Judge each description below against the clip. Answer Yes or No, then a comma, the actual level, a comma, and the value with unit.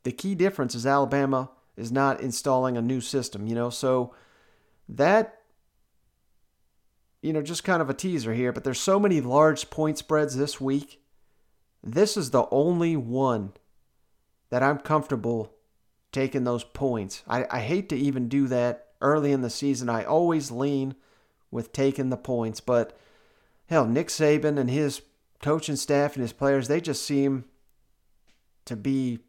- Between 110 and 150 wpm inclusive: No, average, 160 wpm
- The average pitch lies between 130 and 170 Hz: Yes, low, 135 Hz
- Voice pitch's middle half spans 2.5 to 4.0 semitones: Yes, average, 3.5 semitones